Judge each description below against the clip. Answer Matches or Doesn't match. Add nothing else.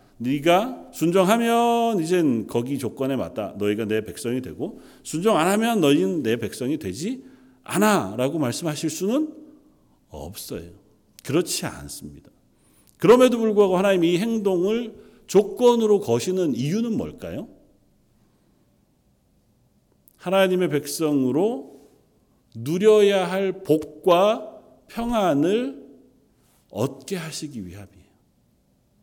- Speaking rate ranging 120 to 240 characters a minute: Matches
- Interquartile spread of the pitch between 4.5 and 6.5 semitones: Doesn't match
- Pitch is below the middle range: Doesn't match